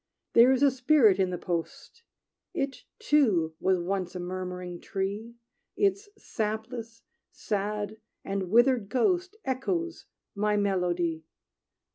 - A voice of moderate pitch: No, high, 210 Hz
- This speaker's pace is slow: Yes, slow, 115 wpm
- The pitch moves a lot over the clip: Yes, wide, 6.0 semitones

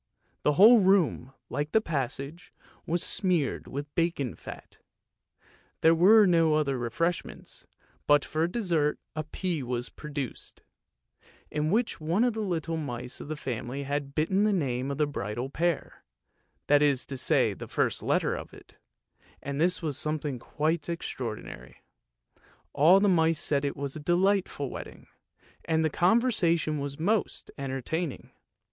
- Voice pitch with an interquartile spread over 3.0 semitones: Yes, average, 3.8 semitones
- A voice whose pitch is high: No, medium, 155 Hz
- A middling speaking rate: Yes, average, 150 wpm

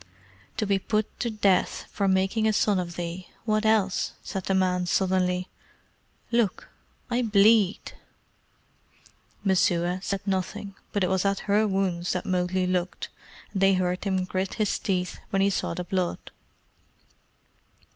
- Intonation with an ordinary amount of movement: No, narrow, 2.0 semitones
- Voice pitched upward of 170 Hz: Yes, high, 190 Hz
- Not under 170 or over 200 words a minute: No, average, 150 wpm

